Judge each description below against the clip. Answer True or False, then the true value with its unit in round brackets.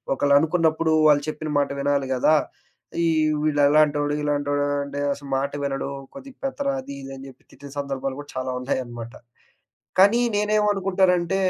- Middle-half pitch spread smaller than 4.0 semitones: False (4.3 semitones)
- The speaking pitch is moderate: True (145 Hz)